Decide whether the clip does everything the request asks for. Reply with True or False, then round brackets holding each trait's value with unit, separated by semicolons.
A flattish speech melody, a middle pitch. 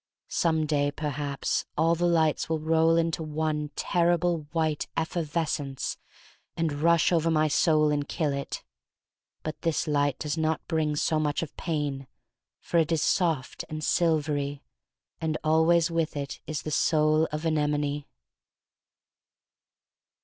True (1.8 semitones; 155 Hz)